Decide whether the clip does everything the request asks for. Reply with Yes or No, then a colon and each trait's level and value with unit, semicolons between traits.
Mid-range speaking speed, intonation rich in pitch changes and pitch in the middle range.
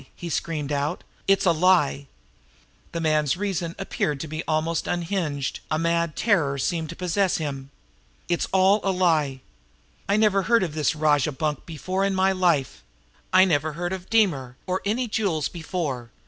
No: average, 165 wpm; average, 3.9 semitones; medium, 170 Hz